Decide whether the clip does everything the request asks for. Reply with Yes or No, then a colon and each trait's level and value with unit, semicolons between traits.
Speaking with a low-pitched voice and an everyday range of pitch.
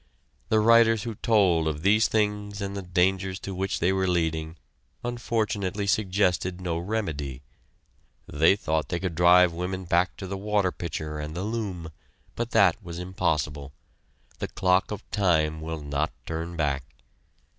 Yes: very low, 90 Hz; average, 3.7 semitones